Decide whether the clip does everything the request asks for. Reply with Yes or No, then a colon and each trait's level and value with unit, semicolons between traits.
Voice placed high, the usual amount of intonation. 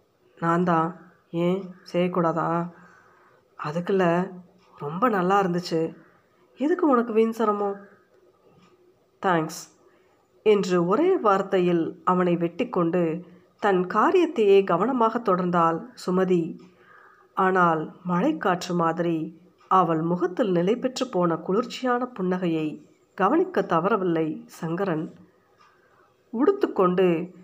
No: medium, 180 Hz; average, 3.9 semitones